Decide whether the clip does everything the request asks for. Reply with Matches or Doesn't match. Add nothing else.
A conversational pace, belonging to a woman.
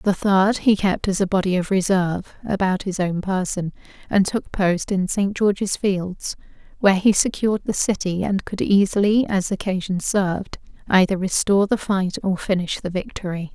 Matches